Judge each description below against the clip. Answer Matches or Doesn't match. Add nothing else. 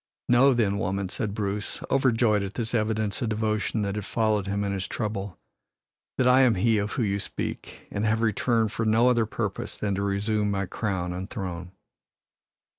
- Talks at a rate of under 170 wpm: Doesn't match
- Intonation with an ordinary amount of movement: Doesn't match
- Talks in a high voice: Doesn't match